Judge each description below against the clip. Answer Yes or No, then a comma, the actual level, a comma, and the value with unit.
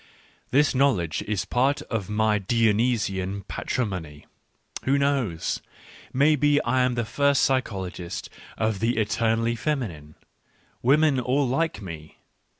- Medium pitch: No, low, 115 Hz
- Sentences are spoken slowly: Yes, slow, 130 wpm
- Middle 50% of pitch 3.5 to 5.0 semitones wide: No, wide, 5.4 semitones